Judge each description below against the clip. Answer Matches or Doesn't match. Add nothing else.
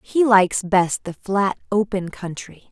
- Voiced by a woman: Matches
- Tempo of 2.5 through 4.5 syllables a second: Matches